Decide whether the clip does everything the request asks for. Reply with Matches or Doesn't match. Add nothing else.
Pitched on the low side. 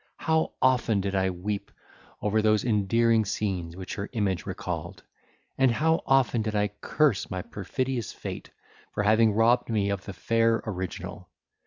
Matches